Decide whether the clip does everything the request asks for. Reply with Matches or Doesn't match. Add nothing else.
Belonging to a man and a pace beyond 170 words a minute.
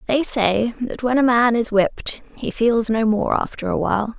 Doesn't match